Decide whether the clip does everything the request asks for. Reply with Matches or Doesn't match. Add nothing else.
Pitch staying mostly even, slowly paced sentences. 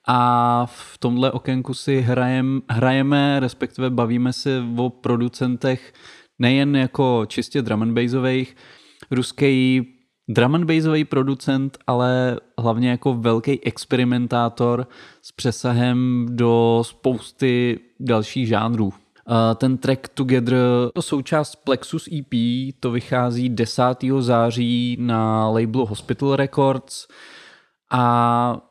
Matches